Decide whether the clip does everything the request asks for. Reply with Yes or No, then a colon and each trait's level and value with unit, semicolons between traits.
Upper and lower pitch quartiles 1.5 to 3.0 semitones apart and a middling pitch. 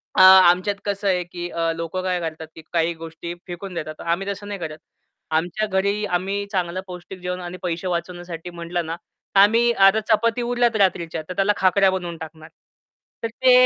Yes: narrow, 2.6 semitones; medium, 180 Hz